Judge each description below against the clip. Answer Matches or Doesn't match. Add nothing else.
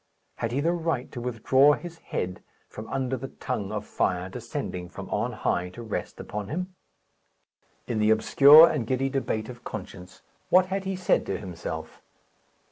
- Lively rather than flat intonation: Matches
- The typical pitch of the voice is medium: Doesn't match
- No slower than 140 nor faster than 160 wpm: Doesn't match